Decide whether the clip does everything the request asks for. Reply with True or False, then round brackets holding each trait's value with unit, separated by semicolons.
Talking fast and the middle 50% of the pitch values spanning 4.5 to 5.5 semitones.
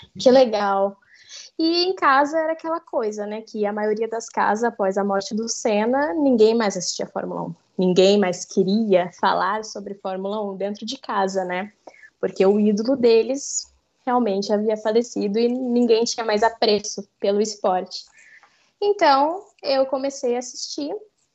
False (155 wpm; 5.2 semitones)